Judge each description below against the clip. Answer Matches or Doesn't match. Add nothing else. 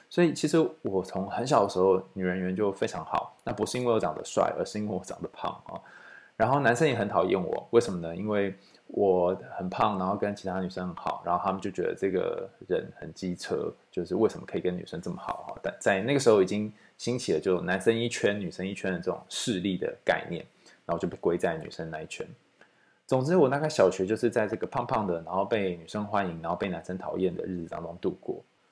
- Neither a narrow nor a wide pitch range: Matches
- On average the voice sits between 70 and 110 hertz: Matches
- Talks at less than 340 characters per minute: Doesn't match